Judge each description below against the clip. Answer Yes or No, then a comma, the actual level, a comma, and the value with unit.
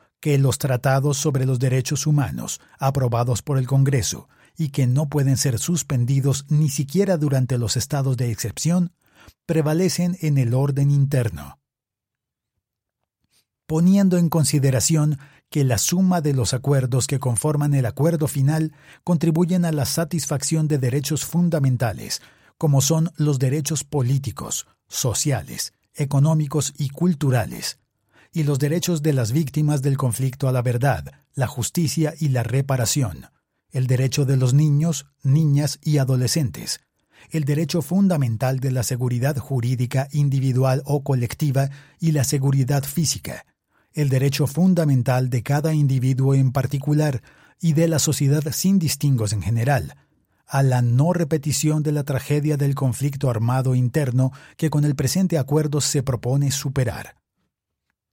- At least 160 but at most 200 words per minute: No, average, 135 wpm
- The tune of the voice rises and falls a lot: No, average, 2.8 semitones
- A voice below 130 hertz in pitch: No, medium, 140 Hz